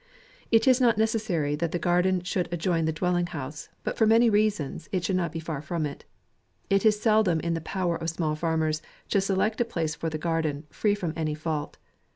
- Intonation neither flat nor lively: Yes, average, 4.3 semitones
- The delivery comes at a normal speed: No, fast, 215 wpm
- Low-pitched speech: No, medium, 170 Hz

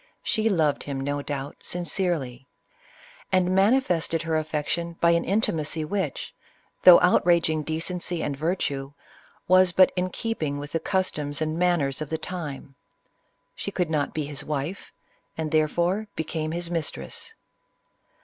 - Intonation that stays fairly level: No, average, 3.3 semitones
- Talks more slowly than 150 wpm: Yes, average, 140 wpm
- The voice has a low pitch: No, medium, 160 Hz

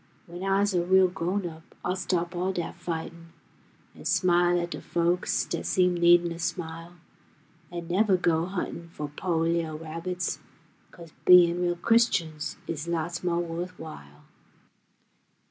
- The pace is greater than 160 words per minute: No, average, 145 wpm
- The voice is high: No, medium, 175 Hz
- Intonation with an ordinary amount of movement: No, narrow, 1.3 semitones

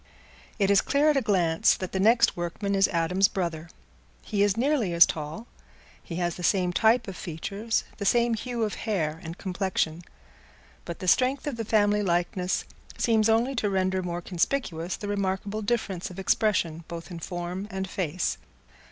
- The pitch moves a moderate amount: Yes, average, 3.9 semitones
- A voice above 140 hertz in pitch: Yes, high, 190 Hz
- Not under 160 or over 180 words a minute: Yes, average, 175 wpm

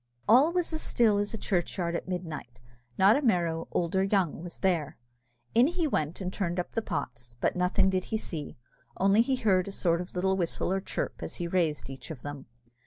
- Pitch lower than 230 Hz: Yes, medium, 185 Hz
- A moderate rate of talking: No, fast, 220 wpm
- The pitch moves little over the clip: No, average, 3.5 semitones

